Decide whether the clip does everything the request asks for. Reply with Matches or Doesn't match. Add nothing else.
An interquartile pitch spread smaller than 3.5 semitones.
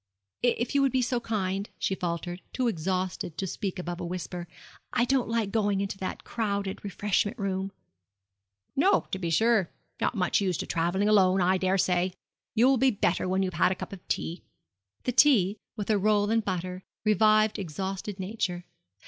Matches